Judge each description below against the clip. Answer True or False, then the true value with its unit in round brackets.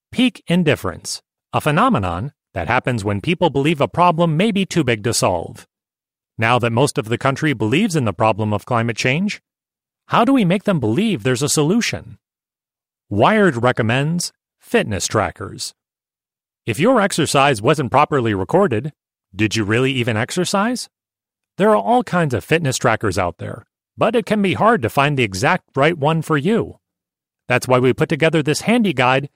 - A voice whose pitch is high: False (140 Hz)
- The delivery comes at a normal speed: True (170 wpm)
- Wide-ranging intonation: True (7.0 semitones)